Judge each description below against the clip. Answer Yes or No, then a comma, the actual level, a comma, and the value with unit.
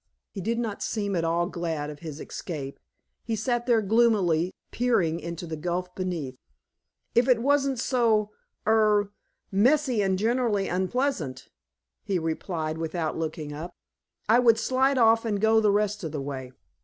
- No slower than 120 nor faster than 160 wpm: Yes, average, 155 wpm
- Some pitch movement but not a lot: No, wide, 5.8 semitones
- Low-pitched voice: No, high, 200 Hz